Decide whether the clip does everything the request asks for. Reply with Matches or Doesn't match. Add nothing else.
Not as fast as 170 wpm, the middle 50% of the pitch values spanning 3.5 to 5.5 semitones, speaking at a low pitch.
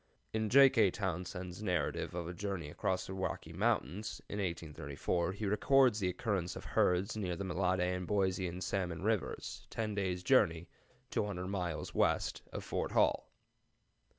Doesn't match